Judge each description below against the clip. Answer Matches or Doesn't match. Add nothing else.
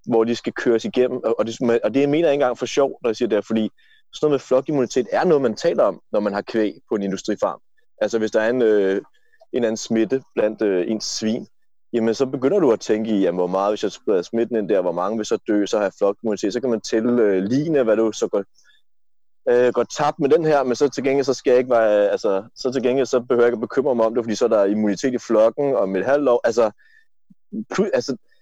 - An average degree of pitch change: Matches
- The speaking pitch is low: Matches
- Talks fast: Matches